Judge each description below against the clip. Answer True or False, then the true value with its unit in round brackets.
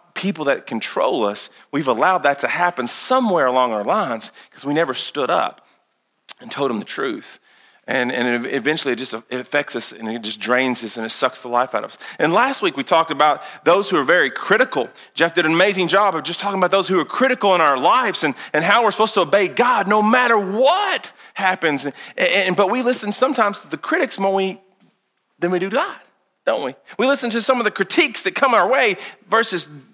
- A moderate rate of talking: False (225 wpm)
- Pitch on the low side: False (180 Hz)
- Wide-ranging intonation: True (8.1 semitones)